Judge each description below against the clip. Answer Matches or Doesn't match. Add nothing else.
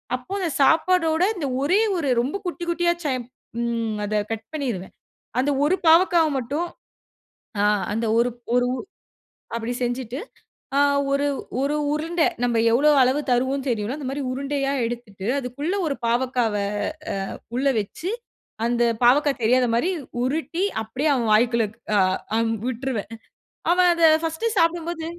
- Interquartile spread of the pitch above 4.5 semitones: Matches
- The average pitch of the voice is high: Matches